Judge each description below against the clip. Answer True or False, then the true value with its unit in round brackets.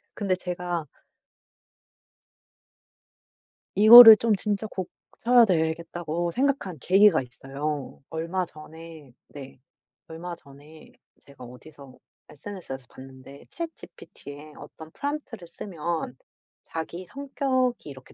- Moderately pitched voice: True (170 Hz)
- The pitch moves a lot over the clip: True (5.7 semitones)